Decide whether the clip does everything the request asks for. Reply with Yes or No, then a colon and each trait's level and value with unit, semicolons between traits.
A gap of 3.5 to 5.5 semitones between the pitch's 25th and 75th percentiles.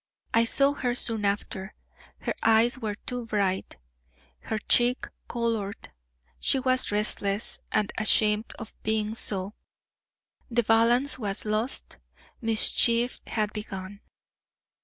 No: narrow, 2.4 semitones